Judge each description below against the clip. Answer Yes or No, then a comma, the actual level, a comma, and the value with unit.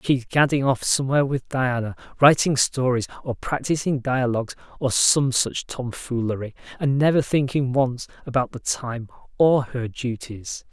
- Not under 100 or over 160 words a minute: Yes, average, 140 wpm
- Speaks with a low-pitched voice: Yes, low, 130 Hz